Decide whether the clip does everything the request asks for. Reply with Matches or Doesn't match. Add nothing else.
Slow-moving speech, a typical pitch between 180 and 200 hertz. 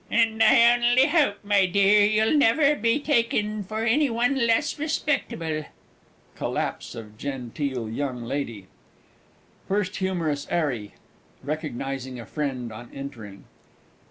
Matches